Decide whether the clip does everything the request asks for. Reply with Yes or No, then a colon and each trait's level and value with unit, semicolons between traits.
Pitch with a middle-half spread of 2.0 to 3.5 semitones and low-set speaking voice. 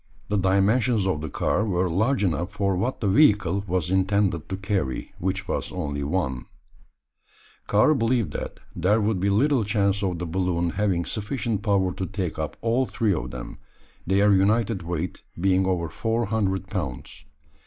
Yes: average, 3.0 semitones; very low, 95 Hz